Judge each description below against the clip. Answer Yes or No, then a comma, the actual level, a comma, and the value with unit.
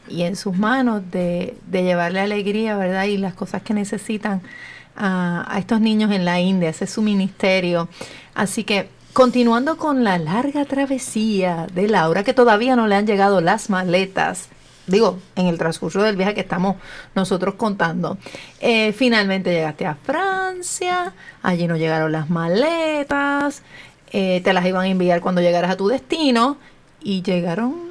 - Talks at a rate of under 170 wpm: Yes, average, 160 wpm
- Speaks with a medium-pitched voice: No, high, 195 Hz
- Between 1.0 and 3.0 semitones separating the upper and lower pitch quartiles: No, average, 4.1 semitones